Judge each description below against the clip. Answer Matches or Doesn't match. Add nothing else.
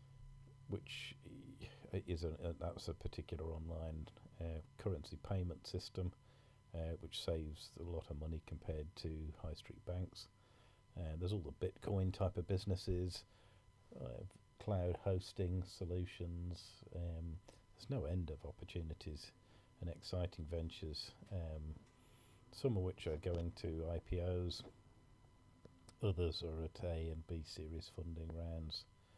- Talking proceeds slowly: Matches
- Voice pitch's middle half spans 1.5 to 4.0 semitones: Doesn't match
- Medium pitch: Doesn't match